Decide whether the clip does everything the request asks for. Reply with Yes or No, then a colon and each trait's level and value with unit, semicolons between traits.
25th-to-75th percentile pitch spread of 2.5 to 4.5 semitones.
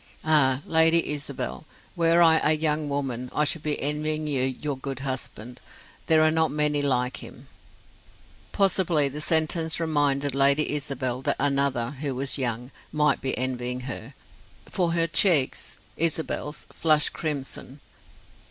Yes: average, 2.9 semitones